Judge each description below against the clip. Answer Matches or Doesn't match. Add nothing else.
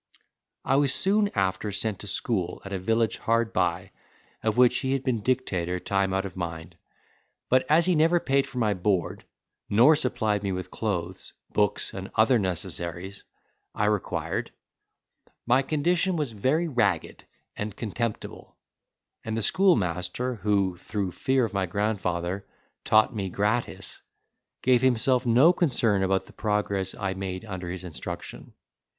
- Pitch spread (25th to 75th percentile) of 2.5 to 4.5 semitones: Doesn't match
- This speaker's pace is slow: Doesn't match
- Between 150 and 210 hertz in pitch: Doesn't match